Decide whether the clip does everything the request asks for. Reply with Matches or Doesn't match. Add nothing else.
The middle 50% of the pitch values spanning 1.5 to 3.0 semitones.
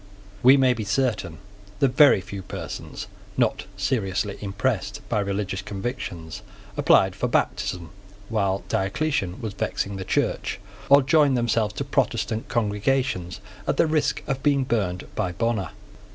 Doesn't match